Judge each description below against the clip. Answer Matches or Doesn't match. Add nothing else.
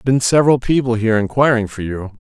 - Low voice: Matches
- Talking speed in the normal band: Matches